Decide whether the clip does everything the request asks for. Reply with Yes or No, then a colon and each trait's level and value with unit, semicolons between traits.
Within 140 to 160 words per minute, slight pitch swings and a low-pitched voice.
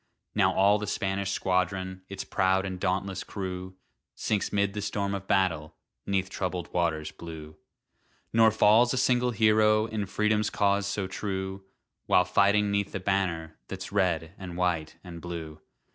Yes: average, 155 wpm; narrow, 2.0 semitones; very low, 95 Hz